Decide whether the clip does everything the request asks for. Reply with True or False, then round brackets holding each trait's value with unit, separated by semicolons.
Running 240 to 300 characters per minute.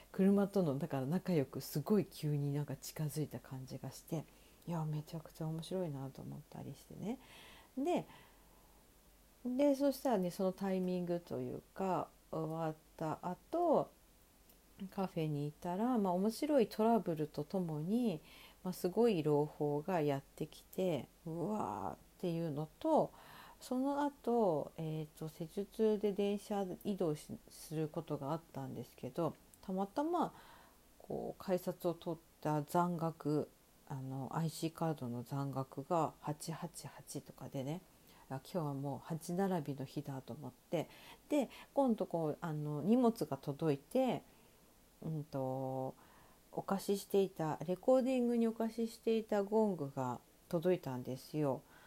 True (270 characters per minute)